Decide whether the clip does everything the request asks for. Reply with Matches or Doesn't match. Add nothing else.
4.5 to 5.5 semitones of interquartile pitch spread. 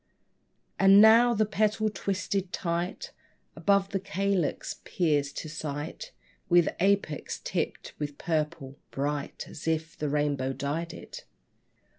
Matches